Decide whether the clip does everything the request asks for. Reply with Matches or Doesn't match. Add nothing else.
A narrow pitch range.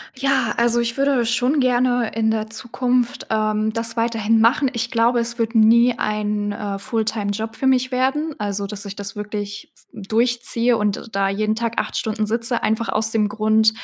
Matches